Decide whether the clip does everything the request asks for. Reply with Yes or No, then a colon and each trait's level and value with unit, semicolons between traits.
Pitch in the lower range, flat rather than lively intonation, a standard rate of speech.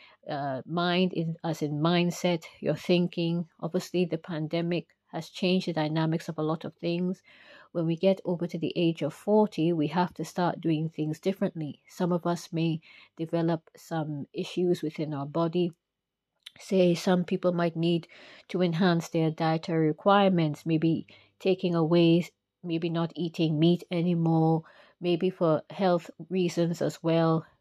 No: medium, 170 Hz; narrow, 1.6 semitones; average, 150 wpm